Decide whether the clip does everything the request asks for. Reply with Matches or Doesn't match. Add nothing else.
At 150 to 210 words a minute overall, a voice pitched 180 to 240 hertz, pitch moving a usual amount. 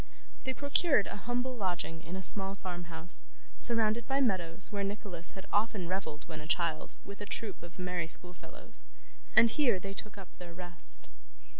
Matches